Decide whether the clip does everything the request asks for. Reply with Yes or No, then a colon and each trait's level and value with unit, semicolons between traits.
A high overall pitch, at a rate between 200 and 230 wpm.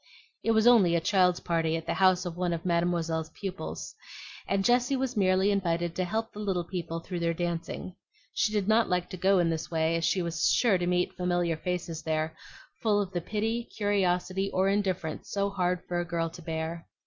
No: medium, 180 Hz; fast, 205 wpm